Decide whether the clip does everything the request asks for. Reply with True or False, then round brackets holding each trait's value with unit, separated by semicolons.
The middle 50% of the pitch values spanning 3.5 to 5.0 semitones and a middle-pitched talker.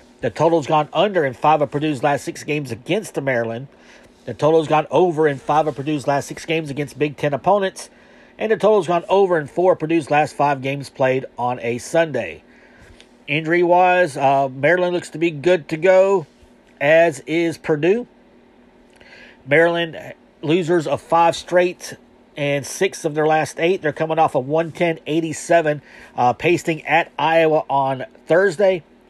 False (3.1 semitones; 155 Hz)